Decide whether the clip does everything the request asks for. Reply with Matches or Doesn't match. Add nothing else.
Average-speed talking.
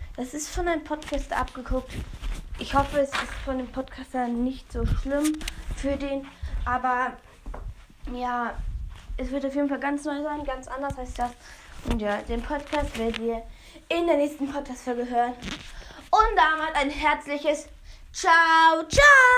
Matches